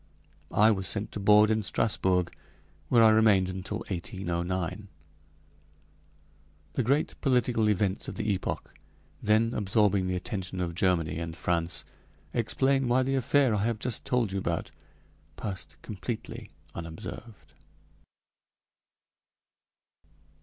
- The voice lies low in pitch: Yes, low, 105 Hz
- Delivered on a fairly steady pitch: No, average, 3.7 semitones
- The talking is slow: Yes, slow, 120 wpm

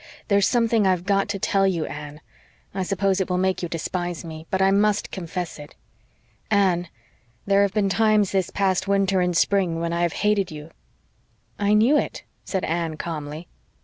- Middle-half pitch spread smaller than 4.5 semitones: Yes, average, 2.8 semitones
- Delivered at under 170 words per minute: No, average, 180 wpm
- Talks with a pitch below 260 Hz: Yes, high, 190 Hz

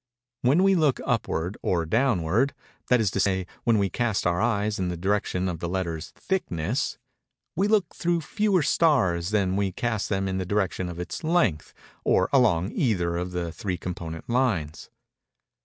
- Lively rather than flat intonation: Yes, wide, 6.1 semitones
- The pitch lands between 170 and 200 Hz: No, low, 100 Hz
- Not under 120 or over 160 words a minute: No, average, 170 wpm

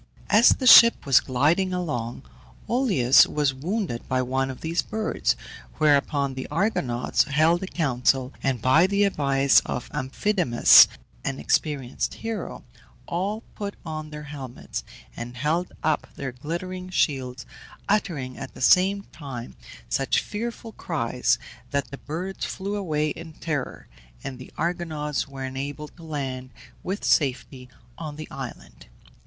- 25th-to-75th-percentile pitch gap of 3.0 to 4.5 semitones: No, wide, 5.5 semitones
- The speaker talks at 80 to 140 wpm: Yes, slow, 135 wpm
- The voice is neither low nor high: Yes, medium, 150 Hz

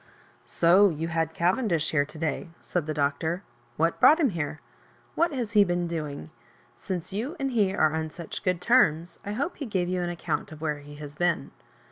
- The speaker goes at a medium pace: No, fast, 220 wpm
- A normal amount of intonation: Yes, average, 4.4 semitones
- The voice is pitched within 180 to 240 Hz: No, medium, 170 Hz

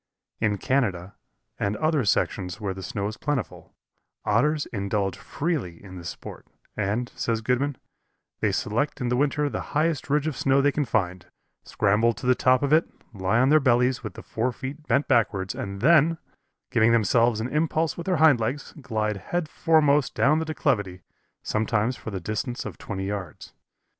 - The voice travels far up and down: Yes, wide, 6.0 semitones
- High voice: No, low, 120 Hz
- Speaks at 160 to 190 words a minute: Yes, average, 170 wpm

